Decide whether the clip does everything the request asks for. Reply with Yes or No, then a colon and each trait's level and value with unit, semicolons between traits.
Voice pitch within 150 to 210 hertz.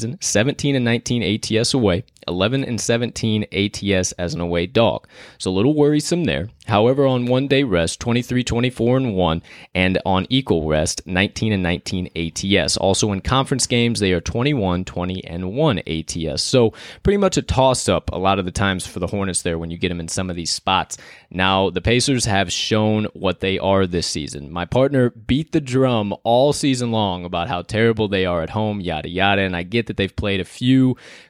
No: low, 100 Hz